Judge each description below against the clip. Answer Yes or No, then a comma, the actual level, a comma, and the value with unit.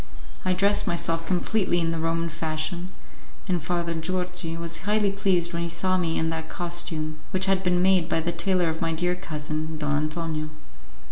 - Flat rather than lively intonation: Yes, narrow, 2.1 semitones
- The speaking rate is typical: Yes, average, 185 wpm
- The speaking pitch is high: No, medium, 170 Hz